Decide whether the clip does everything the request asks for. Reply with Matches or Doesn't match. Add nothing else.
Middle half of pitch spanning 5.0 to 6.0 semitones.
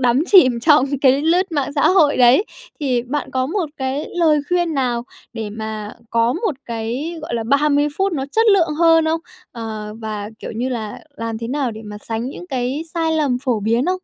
Matches